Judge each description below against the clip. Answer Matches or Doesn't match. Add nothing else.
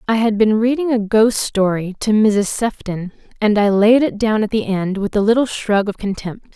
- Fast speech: Matches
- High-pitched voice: Matches